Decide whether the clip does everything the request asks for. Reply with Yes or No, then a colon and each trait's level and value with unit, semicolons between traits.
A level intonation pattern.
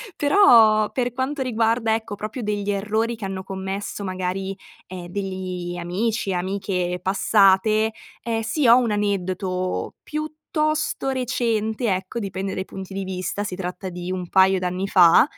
No: average, 3.4 semitones